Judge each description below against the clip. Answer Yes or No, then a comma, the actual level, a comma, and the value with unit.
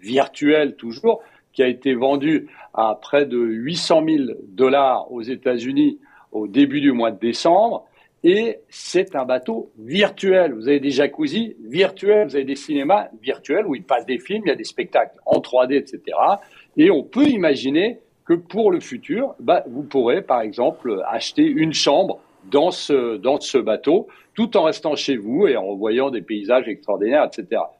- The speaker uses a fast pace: No, average, 175 wpm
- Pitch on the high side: Yes, high, 200 Hz